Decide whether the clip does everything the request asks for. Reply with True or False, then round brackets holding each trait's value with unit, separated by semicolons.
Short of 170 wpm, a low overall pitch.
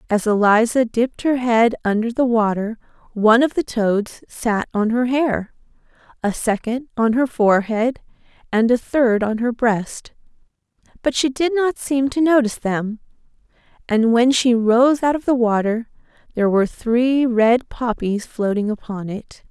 False (155 wpm; 235 Hz)